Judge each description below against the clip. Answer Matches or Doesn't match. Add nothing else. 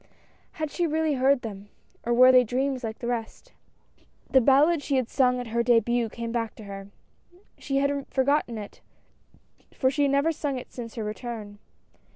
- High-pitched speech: Matches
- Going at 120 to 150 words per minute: Doesn't match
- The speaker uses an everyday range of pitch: Matches